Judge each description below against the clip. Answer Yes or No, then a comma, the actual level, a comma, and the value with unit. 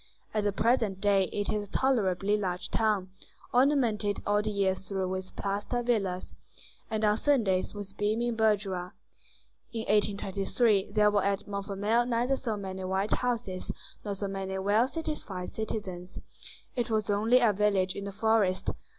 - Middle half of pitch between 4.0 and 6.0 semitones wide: No, narrow, 2.4 semitones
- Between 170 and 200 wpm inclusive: No, average, 155 wpm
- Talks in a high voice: Yes, high, 205 Hz